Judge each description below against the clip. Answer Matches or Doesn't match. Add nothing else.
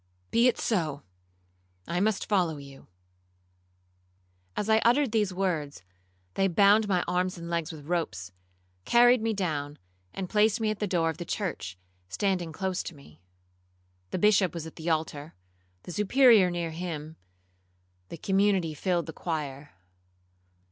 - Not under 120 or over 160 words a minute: Matches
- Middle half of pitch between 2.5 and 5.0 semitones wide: Matches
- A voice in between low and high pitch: Matches